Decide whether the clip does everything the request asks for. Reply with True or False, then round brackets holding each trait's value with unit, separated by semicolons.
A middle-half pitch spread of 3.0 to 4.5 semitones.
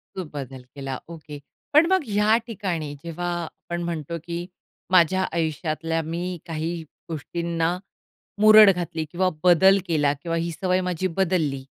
False (2.6 semitones)